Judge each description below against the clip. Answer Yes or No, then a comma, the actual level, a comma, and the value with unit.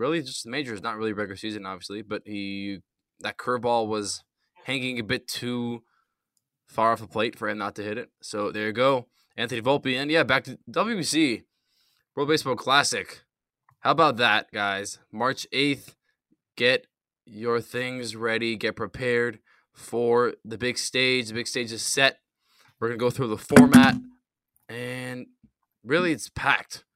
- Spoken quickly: No, average, 165 wpm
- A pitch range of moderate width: Yes, average, 3.1 semitones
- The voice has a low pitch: Yes, low, 120 Hz